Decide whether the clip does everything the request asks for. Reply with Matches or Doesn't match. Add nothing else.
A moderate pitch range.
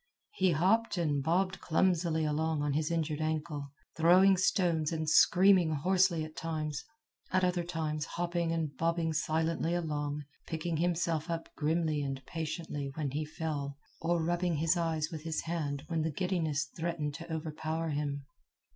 Doesn't match